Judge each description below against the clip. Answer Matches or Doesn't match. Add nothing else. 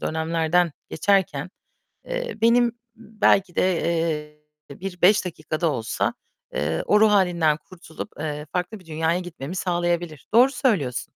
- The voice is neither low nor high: Matches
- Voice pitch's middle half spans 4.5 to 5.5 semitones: Doesn't match